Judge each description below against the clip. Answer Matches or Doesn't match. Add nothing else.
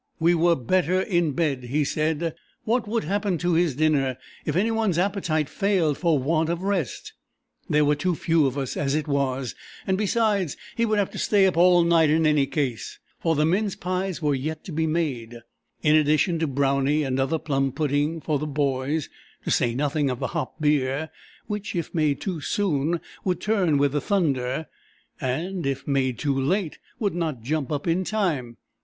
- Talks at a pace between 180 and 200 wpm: Matches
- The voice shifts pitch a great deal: Doesn't match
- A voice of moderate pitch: Matches